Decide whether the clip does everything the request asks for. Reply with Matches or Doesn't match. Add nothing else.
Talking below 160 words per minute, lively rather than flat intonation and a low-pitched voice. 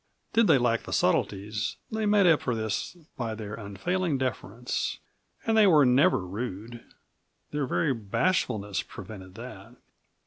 Matches